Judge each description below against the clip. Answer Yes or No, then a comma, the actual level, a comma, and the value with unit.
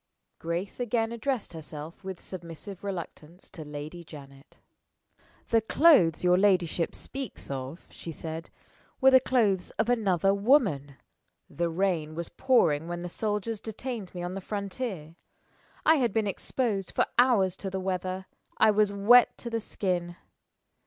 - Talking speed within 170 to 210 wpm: No, average, 145 wpm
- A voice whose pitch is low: No, high, 190 Hz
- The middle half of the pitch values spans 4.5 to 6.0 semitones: Yes, average, 4.9 semitones